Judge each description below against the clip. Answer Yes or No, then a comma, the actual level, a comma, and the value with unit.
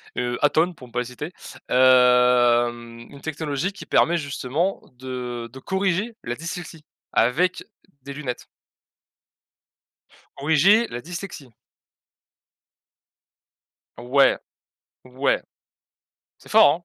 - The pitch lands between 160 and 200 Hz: No, medium, 140 Hz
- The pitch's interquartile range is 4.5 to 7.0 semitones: Yes, average, 5.2 semitones